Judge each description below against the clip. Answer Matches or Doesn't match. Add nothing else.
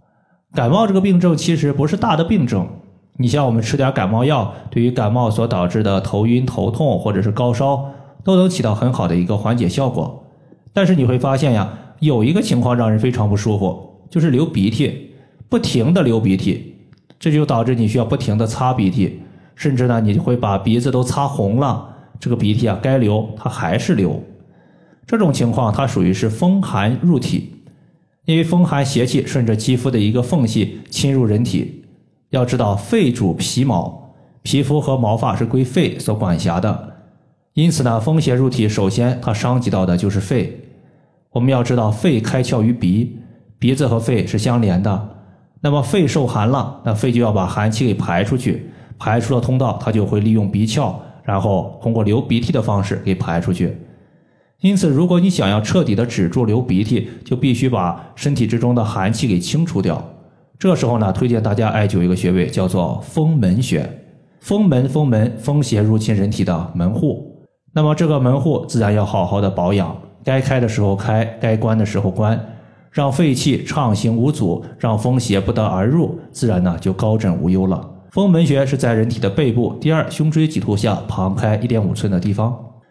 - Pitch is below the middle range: Matches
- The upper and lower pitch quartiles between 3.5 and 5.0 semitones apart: Matches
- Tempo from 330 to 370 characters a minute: Doesn't match